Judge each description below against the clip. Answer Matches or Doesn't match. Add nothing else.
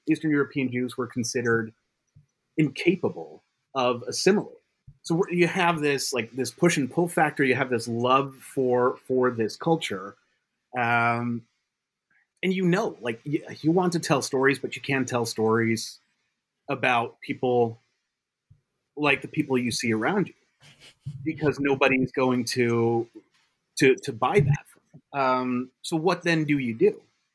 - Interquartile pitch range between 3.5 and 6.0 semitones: Matches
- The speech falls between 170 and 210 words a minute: Doesn't match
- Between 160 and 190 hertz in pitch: Doesn't match